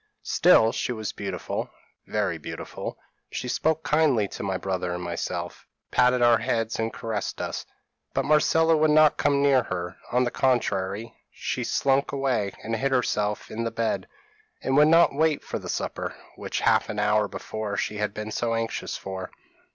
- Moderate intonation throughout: Yes, average, 4.7 semitones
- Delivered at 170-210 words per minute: Yes, average, 175 wpm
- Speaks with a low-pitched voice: Yes, low, 115 Hz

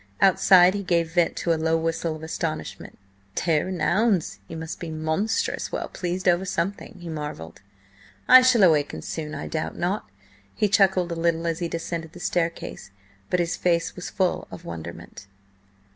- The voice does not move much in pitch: Yes, narrow, 2.2 semitones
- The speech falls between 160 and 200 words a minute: Yes, average, 175 wpm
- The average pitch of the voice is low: No, medium, 170 Hz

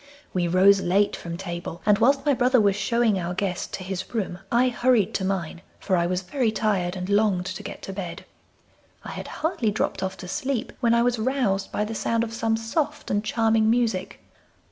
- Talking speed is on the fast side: Yes, fast, 210 wpm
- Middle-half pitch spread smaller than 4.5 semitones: Yes, average, 4.0 semitones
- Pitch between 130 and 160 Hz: No, high, 205 Hz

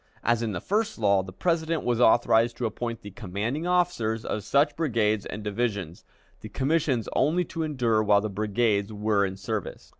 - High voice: No, low, 115 Hz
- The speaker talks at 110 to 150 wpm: No, average, 180 wpm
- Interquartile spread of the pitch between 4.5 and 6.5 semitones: Yes, average, 5.1 semitones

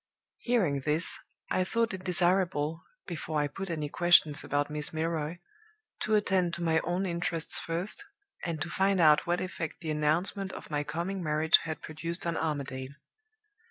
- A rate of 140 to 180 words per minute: Yes, average, 160 wpm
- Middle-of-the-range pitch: Yes, medium, 165 Hz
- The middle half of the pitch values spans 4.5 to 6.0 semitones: No, average, 3.2 semitones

